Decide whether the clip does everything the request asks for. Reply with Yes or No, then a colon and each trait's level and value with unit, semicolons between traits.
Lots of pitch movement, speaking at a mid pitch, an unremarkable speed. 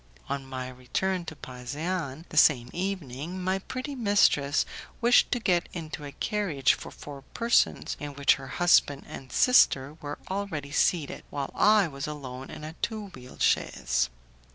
Yes: wide, 5.8 semitones; medium, 150 Hz; average, 155 wpm